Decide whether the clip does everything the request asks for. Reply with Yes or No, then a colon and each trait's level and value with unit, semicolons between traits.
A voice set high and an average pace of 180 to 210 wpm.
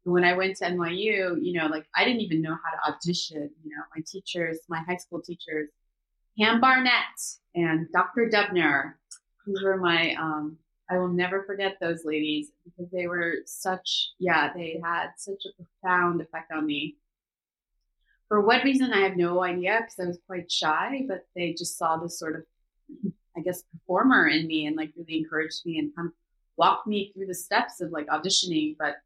No: medium, 175 Hz; average, 190 wpm